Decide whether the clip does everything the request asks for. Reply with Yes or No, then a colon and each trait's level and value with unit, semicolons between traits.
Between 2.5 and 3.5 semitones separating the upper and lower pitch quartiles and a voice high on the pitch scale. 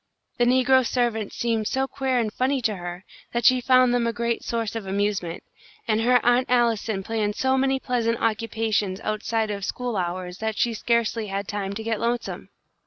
Yes: average, 2.8 semitones; high, 230 Hz